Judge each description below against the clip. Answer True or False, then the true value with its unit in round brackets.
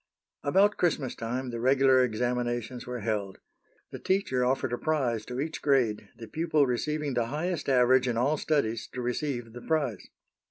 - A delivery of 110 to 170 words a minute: True (165 wpm)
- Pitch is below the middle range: True (125 Hz)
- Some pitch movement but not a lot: True (3.3 semitones)